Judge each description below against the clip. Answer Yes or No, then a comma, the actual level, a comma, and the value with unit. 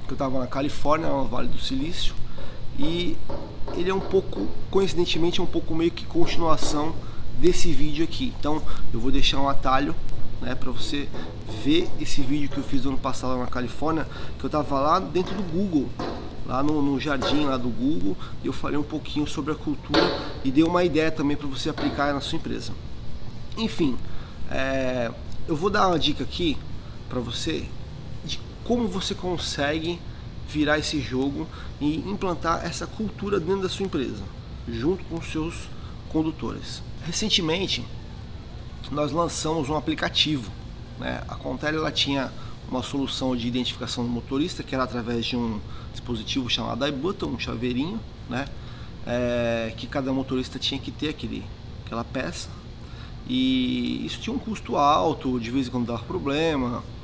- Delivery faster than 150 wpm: Yes, average, 160 wpm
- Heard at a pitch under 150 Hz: Yes, medium, 140 Hz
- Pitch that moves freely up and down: No, average, 4.5 semitones